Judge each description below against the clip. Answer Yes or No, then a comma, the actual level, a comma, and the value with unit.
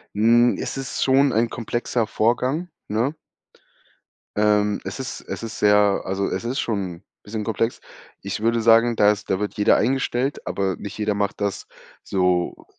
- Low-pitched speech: Yes, low, 110 Hz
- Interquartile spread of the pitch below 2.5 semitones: No, average, 2.8 semitones